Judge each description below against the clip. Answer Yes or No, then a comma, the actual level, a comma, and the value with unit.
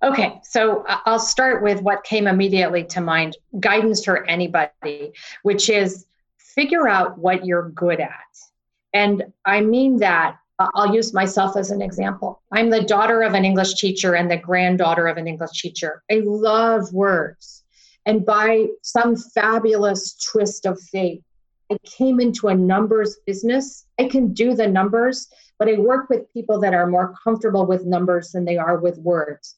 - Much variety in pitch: No, average, 3.6 semitones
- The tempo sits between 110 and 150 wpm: No, average, 165 wpm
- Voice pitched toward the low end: No, high, 200 Hz